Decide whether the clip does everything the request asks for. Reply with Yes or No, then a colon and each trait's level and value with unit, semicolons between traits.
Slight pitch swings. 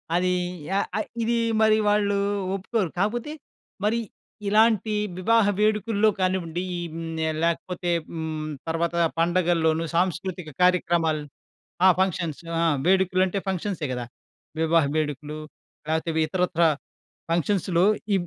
No: average, 3.6 semitones